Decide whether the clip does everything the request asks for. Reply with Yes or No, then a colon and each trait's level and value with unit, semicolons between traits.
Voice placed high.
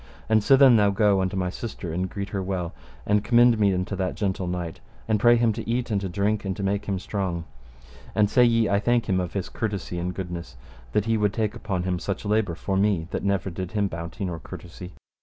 No: low, 100 Hz